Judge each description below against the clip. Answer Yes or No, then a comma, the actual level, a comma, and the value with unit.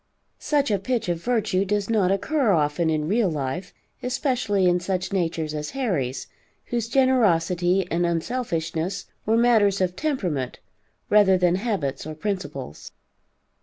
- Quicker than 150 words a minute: No, slow, 135 wpm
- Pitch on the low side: No, high, 190 Hz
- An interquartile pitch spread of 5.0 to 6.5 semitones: Yes, wide, 5.4 semitones